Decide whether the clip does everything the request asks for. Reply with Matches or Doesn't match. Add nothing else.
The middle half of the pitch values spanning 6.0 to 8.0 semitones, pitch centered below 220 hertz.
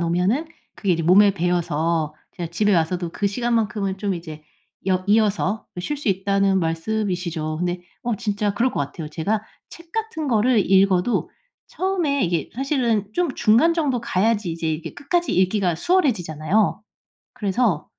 Doesn't match